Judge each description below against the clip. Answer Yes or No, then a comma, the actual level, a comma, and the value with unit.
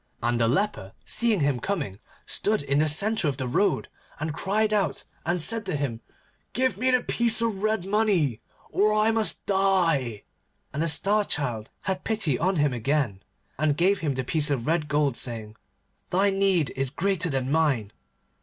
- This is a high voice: No, medium, 165 Hz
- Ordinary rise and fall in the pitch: No, wide, 6.9 semitones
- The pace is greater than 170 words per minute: Yes, average, 180 wpm